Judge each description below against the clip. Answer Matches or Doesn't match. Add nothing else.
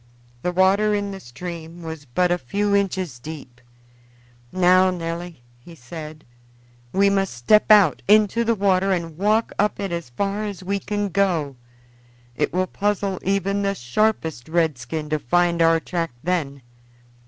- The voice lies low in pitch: Doesn't match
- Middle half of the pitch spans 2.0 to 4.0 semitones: Matches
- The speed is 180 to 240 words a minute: Doesn't match